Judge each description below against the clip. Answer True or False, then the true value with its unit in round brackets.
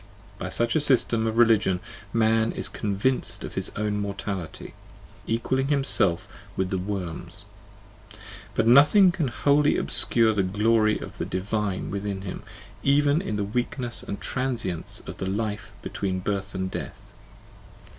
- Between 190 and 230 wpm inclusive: False (145 wpm)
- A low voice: True (105 Hz)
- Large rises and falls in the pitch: False (3.8 semitones)